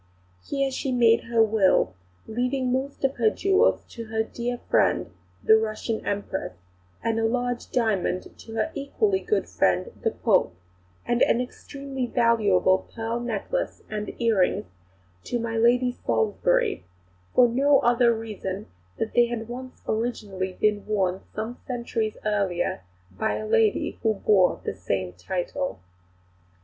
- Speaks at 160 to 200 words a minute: No, slow, 135 wpm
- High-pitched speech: Yes, high, 230 Hz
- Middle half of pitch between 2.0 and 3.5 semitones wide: Yes, average, 3.0 semitones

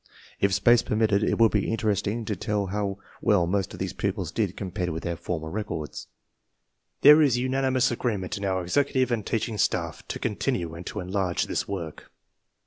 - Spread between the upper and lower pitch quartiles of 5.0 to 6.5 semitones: No, average, 3.8 semitones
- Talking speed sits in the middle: Yes, average, 180 wpm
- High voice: No, low, 100 Hz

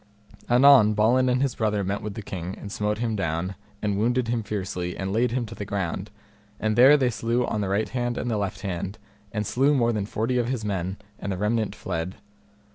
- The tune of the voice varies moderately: Yes, average, 3.5 semitones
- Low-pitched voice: Yes, low, 105 Hz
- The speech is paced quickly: Yes, fast, 220 wpm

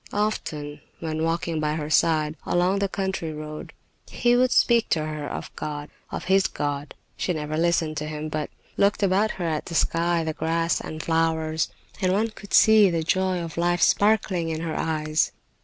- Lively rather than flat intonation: No, average, 3.2 semitones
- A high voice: No, medium, 165 Hz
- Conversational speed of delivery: Yes, average, 185 wpm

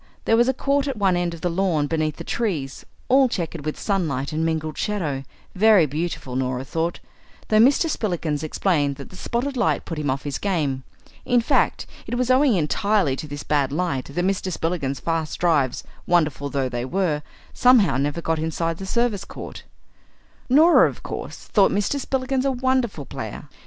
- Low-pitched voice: No, medium, 170 Hz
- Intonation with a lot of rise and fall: Yes, wide, 6.9 semitones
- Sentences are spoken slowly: No, average, 185 wpm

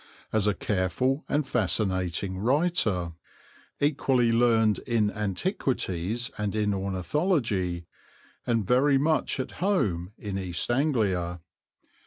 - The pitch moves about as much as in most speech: No, wide, 6.0 semitones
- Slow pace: Yes, slow, 105 wpm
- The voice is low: Yes, low, 110 Hz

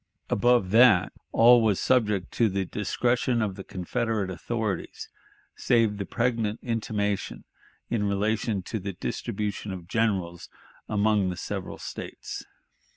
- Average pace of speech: No, slow, 125 wpm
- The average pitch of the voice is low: Yes, low, 105 Hz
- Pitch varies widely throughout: No, average, 3.0 semitones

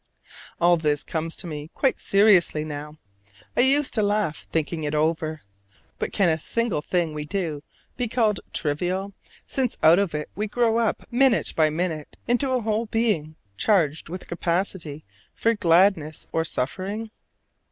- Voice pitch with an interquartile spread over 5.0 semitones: Yes, wide, 5.6 semitones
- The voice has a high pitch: No, medium, 175 Hz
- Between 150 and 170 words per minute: Yes, average, 155 wpm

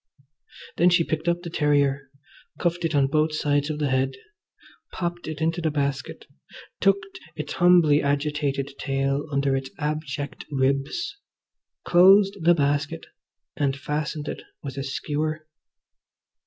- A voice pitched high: No, medium, 150 Hz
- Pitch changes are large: No, average, 2.9 semitones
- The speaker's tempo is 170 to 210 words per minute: No, slow, 135 wpm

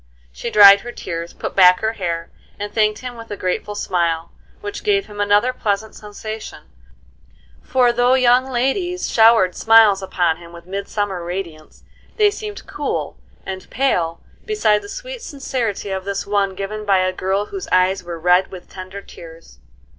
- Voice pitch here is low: No, high, 205 Hz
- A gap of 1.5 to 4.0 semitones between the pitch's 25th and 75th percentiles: No, average, 4.7 semitones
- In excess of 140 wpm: Yes, average, 165 wpm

